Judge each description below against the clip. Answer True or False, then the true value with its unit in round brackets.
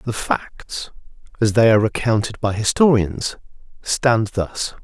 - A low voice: True (110 Hz)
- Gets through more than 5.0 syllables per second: False (3.9 syllables/s)